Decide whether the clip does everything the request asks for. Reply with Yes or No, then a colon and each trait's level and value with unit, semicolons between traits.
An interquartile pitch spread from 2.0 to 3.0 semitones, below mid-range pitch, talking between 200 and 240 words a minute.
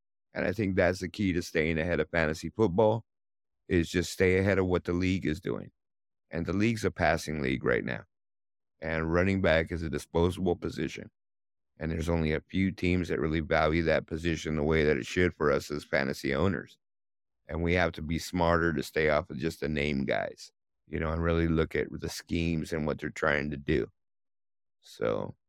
Yes: average, 2.7 semitones; very low, 80 Hz; fast, 205 wpm